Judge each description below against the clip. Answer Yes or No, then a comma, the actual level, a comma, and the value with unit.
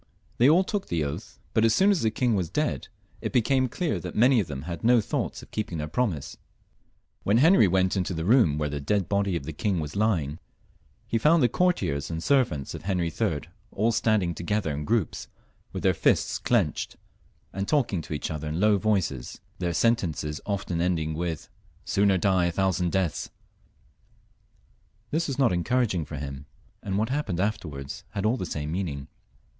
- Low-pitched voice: Yes, very low, 95 Hz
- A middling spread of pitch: No, wide, 6.0 semitones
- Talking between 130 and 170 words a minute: No, average, 190 wpm